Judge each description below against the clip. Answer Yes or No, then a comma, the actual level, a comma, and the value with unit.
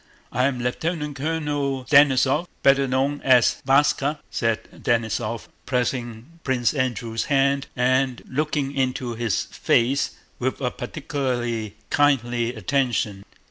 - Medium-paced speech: No, slow, 105 wpm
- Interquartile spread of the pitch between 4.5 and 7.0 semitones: No, average, 2.8 semitones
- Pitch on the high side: No, low, 130 Hz